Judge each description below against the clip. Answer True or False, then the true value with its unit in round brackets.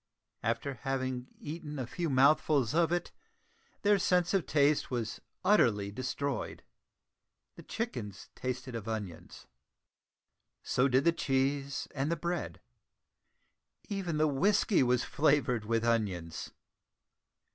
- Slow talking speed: True (115 wpm)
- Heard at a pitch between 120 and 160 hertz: True (135 Hz)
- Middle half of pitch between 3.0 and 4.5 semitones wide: False (4.9 semitones)